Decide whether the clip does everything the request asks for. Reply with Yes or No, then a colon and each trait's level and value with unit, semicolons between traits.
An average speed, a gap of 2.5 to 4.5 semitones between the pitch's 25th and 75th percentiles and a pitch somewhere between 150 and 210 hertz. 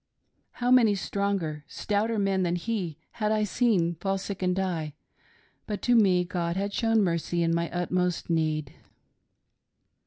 Yes: average, 150 wpm; average, 3.5 semitones; medium, 185 Hz